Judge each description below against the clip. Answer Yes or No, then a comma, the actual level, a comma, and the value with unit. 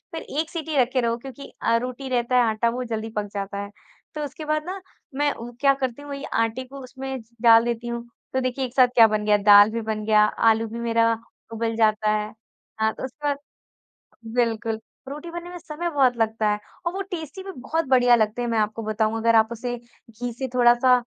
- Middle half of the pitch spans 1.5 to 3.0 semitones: No, average, 3.5 semitones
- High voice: Yes, high, 240 Hz